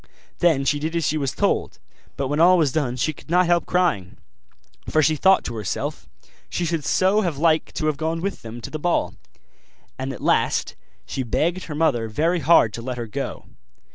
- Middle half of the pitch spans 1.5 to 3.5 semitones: No, average, 4.5 semitones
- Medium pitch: Yes, medium, 155 Hz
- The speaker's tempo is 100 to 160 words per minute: No, fast, 205 wpm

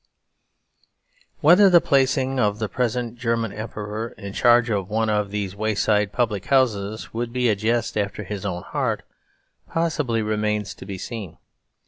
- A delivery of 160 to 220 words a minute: No, average, 150 wpm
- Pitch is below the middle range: Yes, low, 110 Hz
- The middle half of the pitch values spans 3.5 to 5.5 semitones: No, average, 2.8 semitones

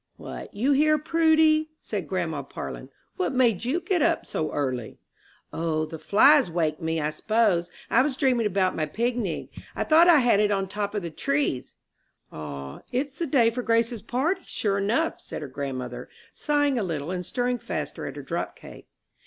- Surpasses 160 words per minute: Yes, average, 185 wpm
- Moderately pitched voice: No, high, 220 Hz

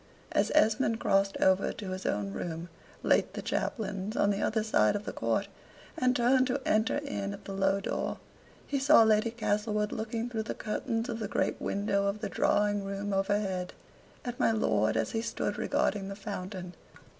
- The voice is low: No, high, 205 Hz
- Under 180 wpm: No, average, 185 wpm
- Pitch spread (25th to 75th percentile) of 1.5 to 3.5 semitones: Yes, narrow, 2.5 semitones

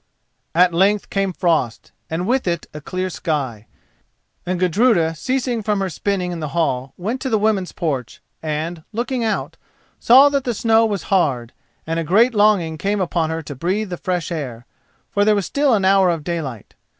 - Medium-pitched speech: Yes, medium, 180 Hz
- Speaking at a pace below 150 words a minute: No, average, 185 wpm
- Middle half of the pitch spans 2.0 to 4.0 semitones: No, average, 4.8 semitones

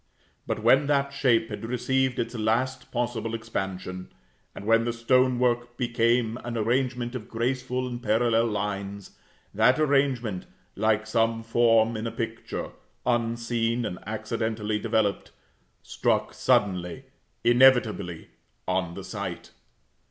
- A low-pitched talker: Yes, low, 115 Hz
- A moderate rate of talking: No, slow, 120 wpm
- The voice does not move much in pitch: Yes, narrow, 2.1 semitones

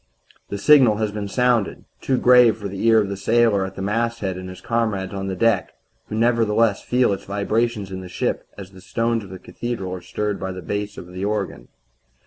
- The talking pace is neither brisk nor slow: No, fast, 215 wpm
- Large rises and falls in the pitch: No, average, 3.2 semitones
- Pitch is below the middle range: Yes, low, 105 Hz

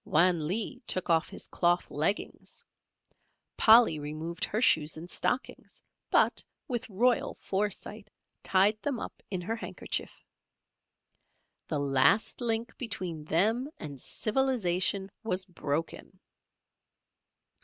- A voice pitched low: No, medium, 185 Hz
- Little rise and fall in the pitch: No, wide, 5.6 semitones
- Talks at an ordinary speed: No, slow, 110 wpm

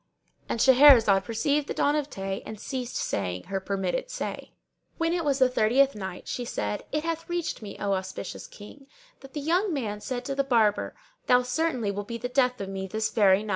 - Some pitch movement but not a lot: No, wide, 5.8 semitones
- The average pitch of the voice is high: Yes, high, 245 Hz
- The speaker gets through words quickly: Yes, fast, 210 wpm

